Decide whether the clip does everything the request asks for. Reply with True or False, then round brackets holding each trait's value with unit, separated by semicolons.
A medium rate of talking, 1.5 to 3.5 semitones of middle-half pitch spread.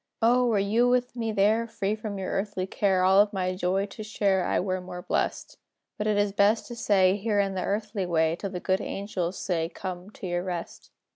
False (220 wpm; 2.5 semitones)